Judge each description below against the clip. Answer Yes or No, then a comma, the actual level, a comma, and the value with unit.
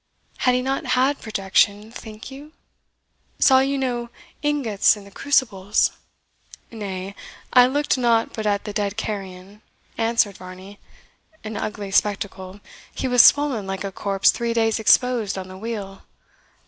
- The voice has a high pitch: Yes, high, 215 Hz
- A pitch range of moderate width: Yes, average, 3.9 semitones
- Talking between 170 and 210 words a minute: No, average, 145 wpm